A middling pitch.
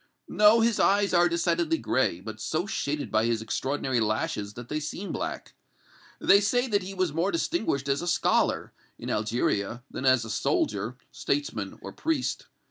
Yes: medium, 145 Hz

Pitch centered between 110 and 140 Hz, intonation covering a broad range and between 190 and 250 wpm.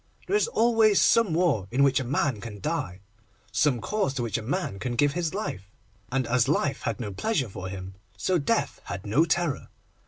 Yes: low, 135 Hz; wide, 8.3 semitones; fast, 205 wpm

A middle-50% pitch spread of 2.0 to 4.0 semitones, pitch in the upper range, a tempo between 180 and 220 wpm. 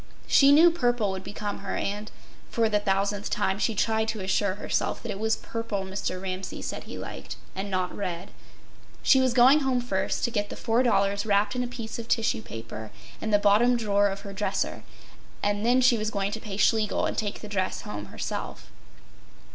Yes: average, 2.9 semitones; high, 210 Hz; average, 195 wpm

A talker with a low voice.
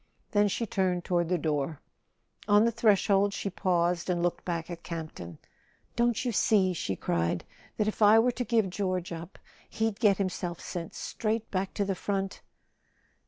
No: high, 190 Hz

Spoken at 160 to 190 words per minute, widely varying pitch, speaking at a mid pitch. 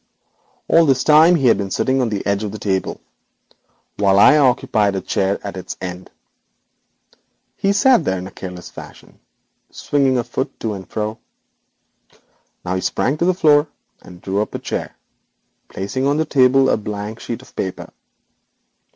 No: average, 170 wpm; wide, 6.2 semitones; low, 110 Hz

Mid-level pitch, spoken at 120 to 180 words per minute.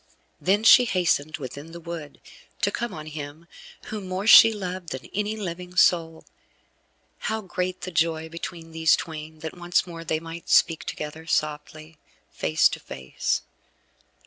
Yes: medium, 165 Hz; average, 150 wpm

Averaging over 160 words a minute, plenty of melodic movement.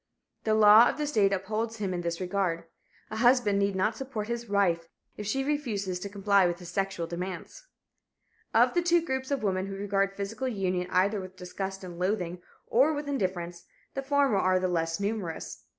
No: average, 190 wpm; average, 3.8 semitones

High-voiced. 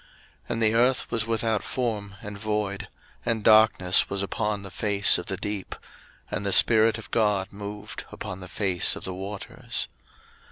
No: low, 105 Hz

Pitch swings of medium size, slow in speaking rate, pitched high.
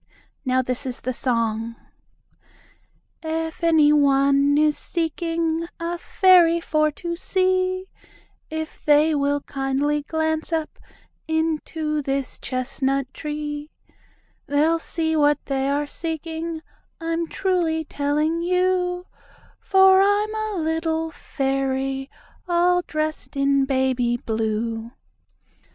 Yes: average, 3.4 semitones; slow, 105 wpm; very high, 310 Hz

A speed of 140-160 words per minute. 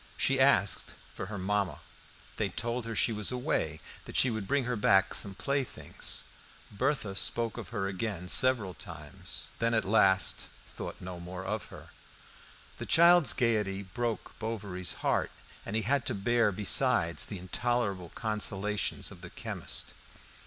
Yes: average, 150 wpm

